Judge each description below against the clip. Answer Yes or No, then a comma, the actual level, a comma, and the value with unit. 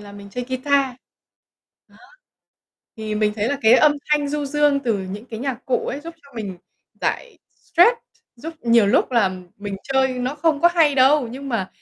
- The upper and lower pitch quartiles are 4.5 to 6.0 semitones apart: Yes, average, 5.0 semitones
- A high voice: Yes, very high, 260 Hz